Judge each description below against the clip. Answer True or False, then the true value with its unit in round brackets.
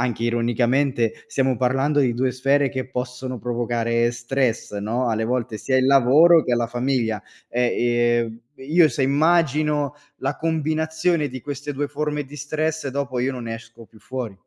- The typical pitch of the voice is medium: False (130 Hz)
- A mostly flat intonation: False (3.4 semitones)